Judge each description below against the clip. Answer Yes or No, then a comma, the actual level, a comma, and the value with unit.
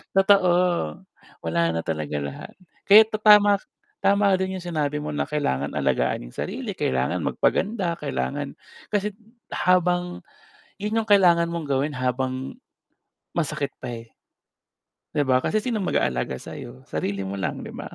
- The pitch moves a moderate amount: No, wide, 8.3 semitones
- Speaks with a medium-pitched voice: Yes, medium, 150 Hz